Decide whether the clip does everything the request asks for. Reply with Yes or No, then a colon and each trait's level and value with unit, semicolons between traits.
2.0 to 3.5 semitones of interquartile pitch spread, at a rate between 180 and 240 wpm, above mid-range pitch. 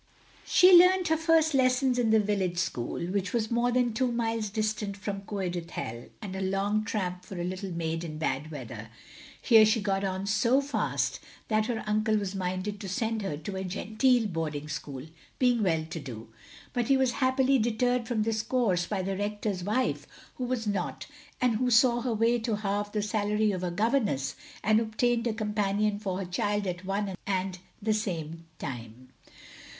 No: average, 4.0 semitones; average, 185 wpm; high, 210 Hz